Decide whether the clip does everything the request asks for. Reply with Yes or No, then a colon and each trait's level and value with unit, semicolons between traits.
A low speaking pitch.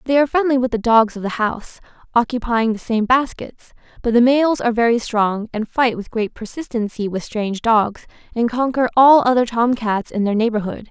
No: high, 230 Hz